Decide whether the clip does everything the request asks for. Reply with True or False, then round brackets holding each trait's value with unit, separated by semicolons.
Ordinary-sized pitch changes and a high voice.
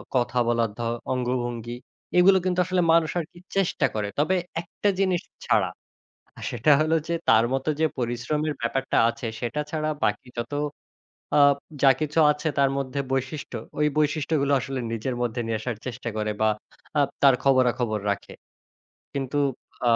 False (4.3 semitones; 135 Hz)